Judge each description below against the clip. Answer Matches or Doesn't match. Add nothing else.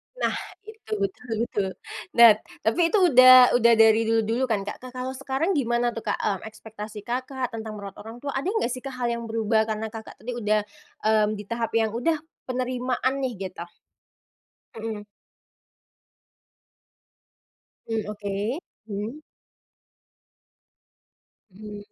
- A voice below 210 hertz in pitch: Doesn't match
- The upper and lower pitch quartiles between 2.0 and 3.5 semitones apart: Matches